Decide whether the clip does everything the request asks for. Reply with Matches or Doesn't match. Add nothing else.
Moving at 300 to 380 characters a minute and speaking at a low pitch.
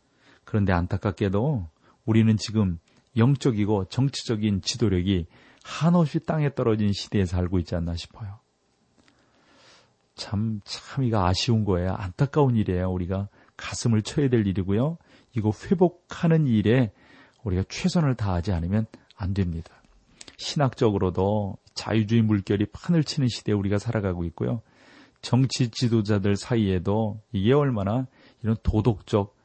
Matches